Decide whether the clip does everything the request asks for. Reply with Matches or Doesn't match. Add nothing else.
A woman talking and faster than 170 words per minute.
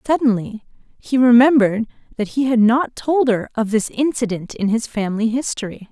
Doesn't match